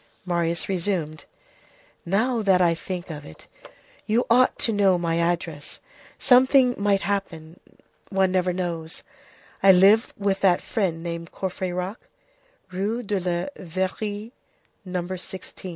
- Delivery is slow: Yes, slow, 125 wpm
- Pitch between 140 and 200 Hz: Yes, medium, 185 Hz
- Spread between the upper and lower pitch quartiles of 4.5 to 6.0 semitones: No, average, 2.9 semitones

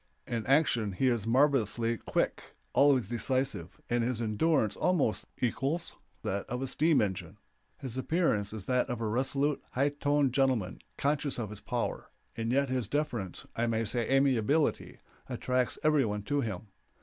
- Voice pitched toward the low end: Yes, low, 125 Hz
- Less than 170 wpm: Yes, average, 160 wpm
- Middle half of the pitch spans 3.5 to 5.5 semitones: Yes, average, 4.1 semitones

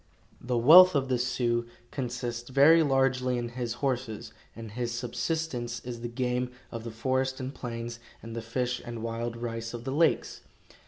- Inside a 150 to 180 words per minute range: Yes, average, 170 wpm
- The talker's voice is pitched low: Yes, low, 120 Hz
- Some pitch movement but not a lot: No, narrow, 2.0 semitones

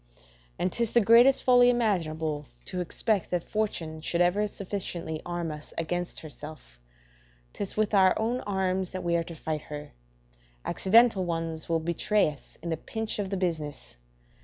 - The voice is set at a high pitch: No, medium, 175 Hz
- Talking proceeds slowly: No, average, 160 wpm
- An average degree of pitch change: Yes, average, 4.6 semitones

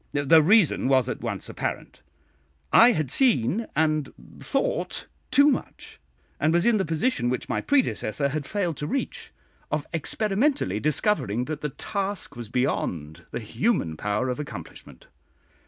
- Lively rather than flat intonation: Yes, wide, 8.6 semitones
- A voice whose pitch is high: No, medium, 150 Hz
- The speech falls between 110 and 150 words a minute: Yes, average, 145 wpm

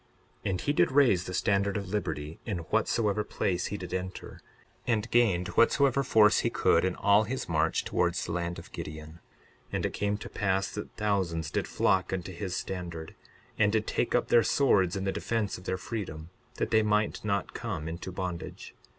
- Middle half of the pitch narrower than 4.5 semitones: Yes, average, 3.2 semitones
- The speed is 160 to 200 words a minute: Yes, average, 195 wpm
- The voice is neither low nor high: No, low, 100 Hz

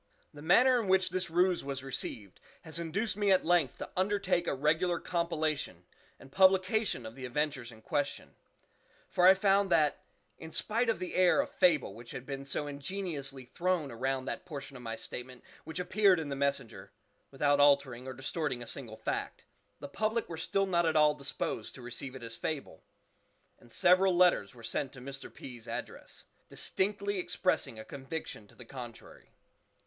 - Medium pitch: Yes, medium, 150 Hz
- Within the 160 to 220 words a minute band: Yes, average, 180 wpm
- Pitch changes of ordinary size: No, wide, 5.9 semitones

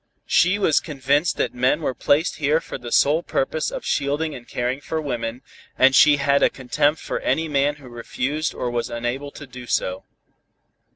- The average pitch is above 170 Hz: No, medium, 140 Hz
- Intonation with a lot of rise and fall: No, average, 3.4 semitones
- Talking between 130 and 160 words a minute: No, average, 185 wpm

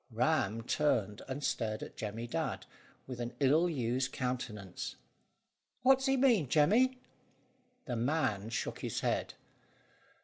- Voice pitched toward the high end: No, low, 130 Hz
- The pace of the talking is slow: Yes, slow, 130 wpm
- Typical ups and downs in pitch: No, wide, 5.8 semitones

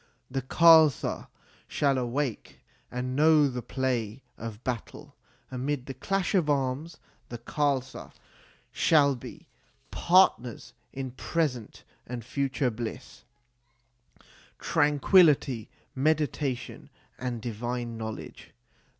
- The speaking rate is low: Yes, slow, 105 wpm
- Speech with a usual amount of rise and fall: Yes, average, 3.3 semitones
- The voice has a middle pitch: No, low, 130 Hz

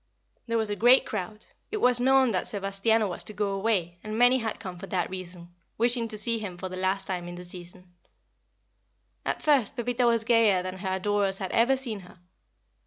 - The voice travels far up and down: No, average, 3.9 semitones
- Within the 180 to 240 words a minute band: Yes, fast, 205 wpm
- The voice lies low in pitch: No, high, 205 Hz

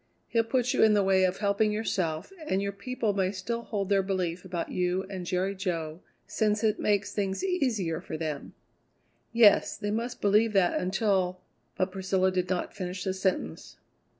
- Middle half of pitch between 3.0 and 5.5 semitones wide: No, narrow, 2.5 semitones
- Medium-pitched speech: No, high, 195 Hz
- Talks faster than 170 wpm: Yes, average, 180 wpm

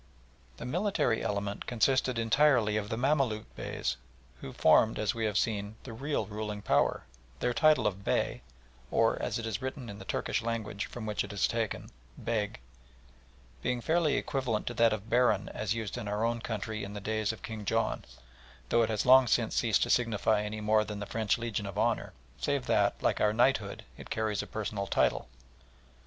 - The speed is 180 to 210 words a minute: Yes, average, 190 wpm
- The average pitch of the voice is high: No, low, 110 Hz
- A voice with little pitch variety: Yes, narrow, 2.3 semitones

